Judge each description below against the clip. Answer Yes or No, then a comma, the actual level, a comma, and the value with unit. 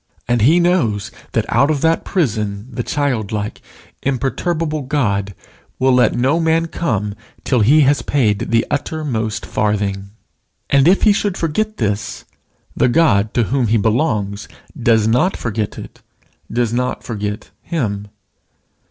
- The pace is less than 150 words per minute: Yes, average, 140 wpm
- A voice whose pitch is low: Yes, low, 120 Hz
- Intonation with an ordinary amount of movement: No, wide, 6.3 semitones